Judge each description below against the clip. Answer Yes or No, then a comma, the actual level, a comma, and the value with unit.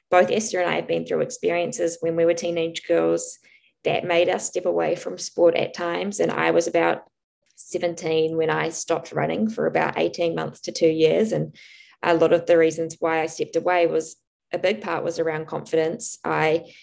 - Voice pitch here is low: No, medium, 165 Hz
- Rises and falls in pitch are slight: Yes, narrow, 1.2 semitones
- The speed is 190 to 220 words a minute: Yes, average, 200 wpm